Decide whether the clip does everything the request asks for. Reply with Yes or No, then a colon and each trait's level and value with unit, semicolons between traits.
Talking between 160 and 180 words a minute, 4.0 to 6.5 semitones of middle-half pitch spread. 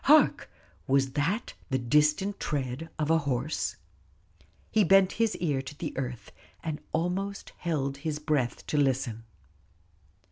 No: slow, 135 wpm; average, 4.3 semitones